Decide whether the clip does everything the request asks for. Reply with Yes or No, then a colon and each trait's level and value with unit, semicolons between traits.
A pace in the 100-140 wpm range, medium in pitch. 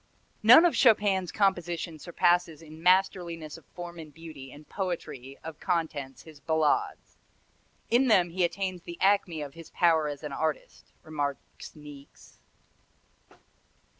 Yes: slow, 135 wpm; medium, 165 Hz